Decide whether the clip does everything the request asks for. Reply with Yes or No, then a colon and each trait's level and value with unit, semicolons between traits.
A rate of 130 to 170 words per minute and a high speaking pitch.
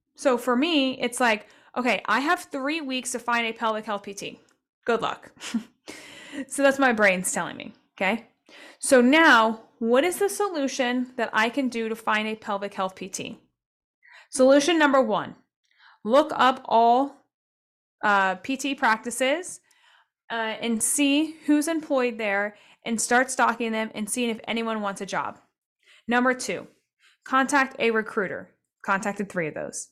Yes: average, 150 wpm; high, 245 Hz